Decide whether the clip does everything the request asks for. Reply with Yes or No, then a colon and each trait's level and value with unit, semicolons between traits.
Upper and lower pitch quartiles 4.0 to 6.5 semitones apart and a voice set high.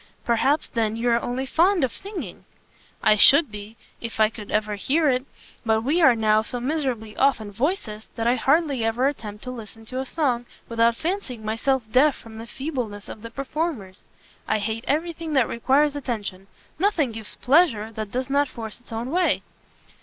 Yes: average, 4.4 semitones; high, 245 Hz